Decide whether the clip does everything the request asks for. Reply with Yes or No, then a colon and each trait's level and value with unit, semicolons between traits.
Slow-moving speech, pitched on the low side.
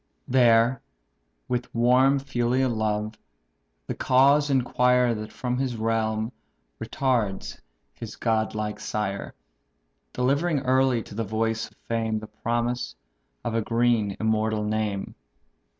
Yes: slow, 120 wpm; low, 115 Hz